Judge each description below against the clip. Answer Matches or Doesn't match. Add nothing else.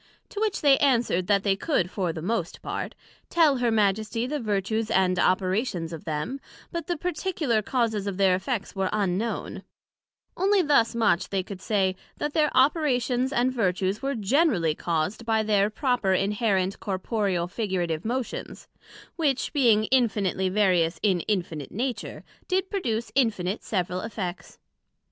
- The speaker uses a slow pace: Doesn't match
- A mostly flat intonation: Doesn't match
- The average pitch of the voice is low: Doesn't match